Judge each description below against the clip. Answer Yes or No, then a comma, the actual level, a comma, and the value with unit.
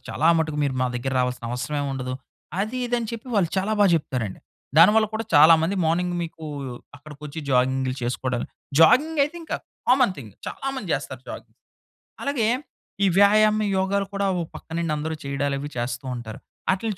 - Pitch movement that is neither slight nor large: No, wide, 7.6 semitones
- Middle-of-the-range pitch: Yes, medium, 160 Hz